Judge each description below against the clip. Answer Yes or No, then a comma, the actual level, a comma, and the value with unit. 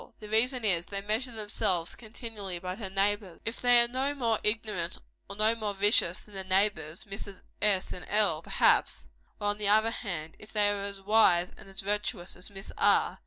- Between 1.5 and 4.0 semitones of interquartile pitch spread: Yes, narrow, 2.4 semitones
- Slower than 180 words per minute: No, average, 200 wpm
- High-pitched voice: Yes, high, 205 Hz